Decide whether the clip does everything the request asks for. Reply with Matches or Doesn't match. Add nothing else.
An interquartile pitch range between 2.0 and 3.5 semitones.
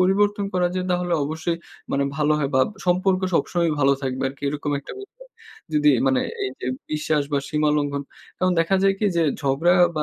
Doesn't match